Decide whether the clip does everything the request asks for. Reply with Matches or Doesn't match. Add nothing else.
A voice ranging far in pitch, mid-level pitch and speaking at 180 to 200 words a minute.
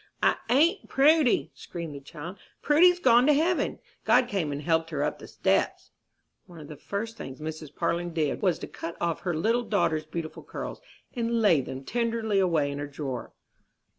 Matches